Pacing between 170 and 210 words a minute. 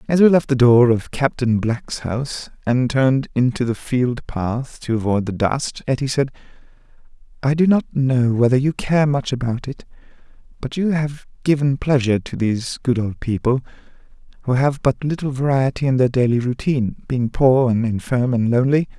Yes: average, 175 wpm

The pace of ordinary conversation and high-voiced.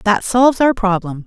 Yes: average, 190 wpm; high, 210 Hz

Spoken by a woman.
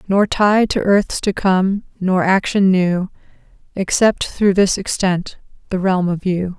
Yes: female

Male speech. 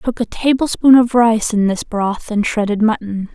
No: female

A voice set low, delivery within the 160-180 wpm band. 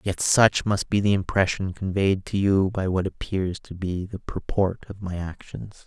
No: very low, 95 Hz; average, 195 wpm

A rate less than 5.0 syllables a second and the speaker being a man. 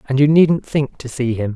Yes: 4.8 syllables/s; male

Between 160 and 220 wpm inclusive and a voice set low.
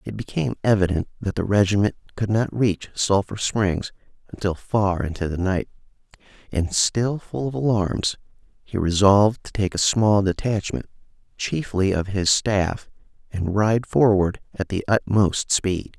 No: average, 145 wpm; low, 100 Hz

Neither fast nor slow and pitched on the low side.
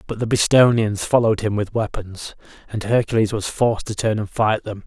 Yes: average, 195 wpm; low, 110 Hz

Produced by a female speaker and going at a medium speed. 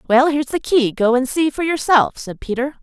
No: female; fast, 210 wpm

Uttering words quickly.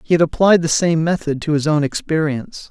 Yes: fast, 220 wpm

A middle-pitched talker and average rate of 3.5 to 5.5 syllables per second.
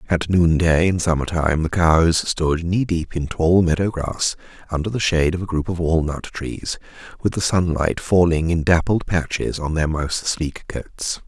No: very low, 85 Hz; 4.6 syllables/s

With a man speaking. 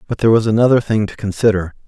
Yes: male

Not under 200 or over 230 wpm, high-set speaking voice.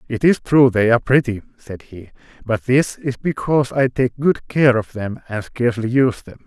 No: fast, 205 wpm; low, 120 Hz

